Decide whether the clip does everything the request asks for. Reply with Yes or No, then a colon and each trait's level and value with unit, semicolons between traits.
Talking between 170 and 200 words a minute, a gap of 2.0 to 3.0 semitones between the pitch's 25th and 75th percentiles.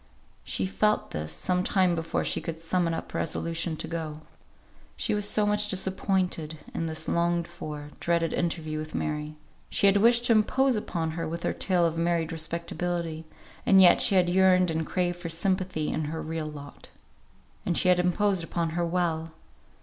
Yes: average, 180 wpm; narrow, 2.5 semitones